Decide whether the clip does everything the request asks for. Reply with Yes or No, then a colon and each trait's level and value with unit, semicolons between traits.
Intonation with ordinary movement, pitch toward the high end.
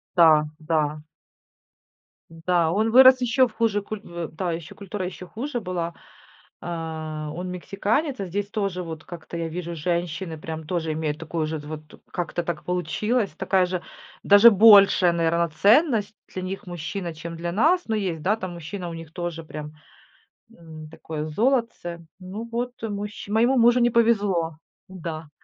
No: average, 4.2 semitones; medium, 180 Hz